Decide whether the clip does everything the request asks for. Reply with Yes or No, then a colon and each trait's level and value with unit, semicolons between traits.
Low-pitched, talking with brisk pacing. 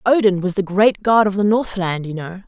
No: high, 195 Hz; fast, 245 wpm